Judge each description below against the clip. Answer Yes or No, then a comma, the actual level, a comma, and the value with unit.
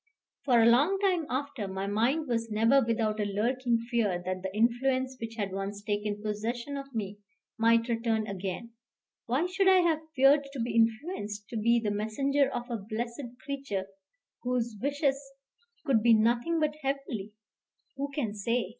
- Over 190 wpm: No, average, 165 wpm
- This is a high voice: Yes, high, 235 Hz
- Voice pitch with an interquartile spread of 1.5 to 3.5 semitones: No, average, 4.4 semitones